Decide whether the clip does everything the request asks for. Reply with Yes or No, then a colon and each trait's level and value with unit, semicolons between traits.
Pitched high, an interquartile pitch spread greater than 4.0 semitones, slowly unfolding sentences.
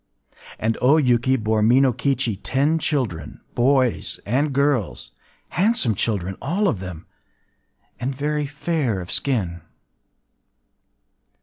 No: low, 130 Hz; average, 5.1 semitones; slow, 100 wpm